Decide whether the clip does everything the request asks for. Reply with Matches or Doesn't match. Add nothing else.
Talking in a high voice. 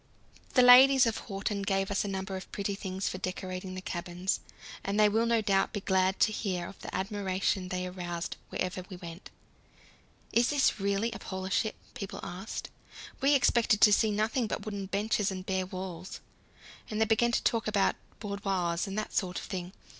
Matches